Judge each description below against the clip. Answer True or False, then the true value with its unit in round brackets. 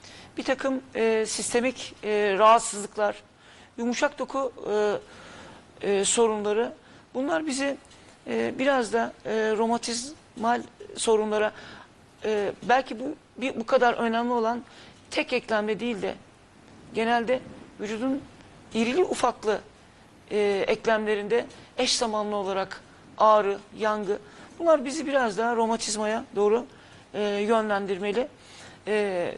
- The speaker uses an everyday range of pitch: True (3.2 semitones)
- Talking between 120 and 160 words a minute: False (100 wpm)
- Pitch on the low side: False (230 Hz)